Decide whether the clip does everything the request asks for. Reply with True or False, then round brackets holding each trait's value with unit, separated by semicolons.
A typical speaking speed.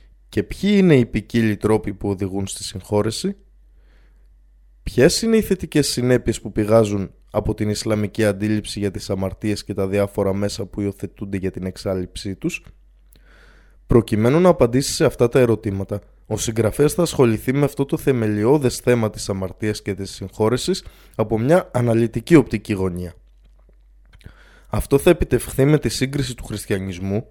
True (150 wpm)